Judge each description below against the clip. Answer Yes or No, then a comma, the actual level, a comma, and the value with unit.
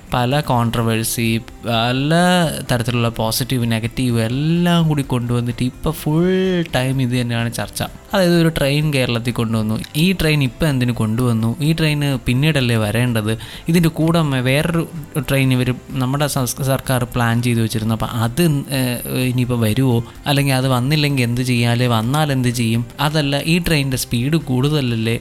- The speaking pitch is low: Yes, low, 130 Hz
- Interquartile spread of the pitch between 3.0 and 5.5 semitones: Yes, average, 4.1 semitones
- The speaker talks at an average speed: No, fast, 130 wpm